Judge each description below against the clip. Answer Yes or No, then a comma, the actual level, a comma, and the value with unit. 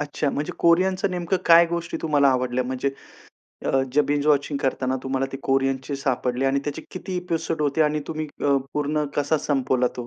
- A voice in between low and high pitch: Yes, medium, 145 Hz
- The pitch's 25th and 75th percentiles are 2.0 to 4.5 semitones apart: Yes, average, 3.3 semitones